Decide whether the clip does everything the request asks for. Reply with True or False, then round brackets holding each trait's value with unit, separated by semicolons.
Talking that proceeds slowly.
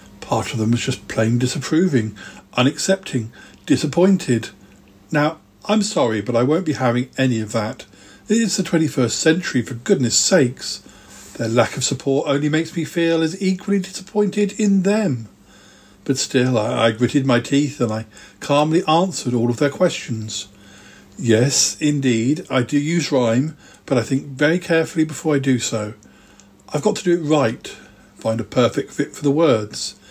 False (165 wpm)